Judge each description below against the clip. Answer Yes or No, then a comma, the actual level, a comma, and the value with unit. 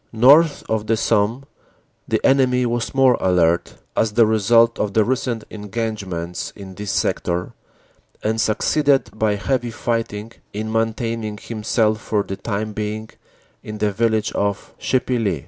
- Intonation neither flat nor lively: No, narrow, 2.1 semitones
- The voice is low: Yes, low, 110 Hz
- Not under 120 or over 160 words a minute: Yes, average, 145 wpm